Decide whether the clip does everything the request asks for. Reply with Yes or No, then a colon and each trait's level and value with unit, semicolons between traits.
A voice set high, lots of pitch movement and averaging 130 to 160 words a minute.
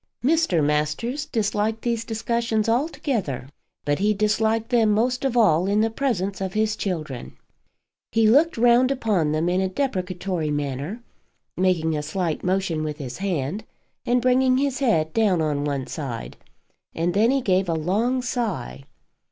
Yes: high, 200 Hz; wide, 6.6 semitones; average, 150 wpm